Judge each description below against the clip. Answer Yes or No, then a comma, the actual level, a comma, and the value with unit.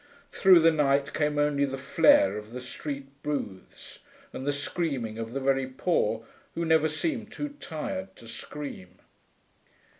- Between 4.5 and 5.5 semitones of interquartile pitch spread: Yes, average, 5.0 semitones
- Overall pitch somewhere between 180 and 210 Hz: No, medium, 140 Hz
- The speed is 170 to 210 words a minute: No, average, 150 wpm